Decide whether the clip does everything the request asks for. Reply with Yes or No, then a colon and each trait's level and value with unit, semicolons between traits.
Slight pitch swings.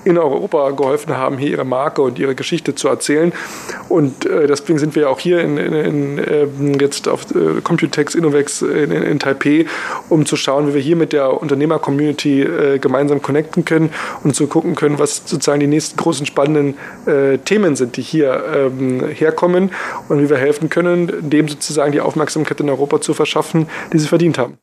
Yes: narrow, 2.1 semitones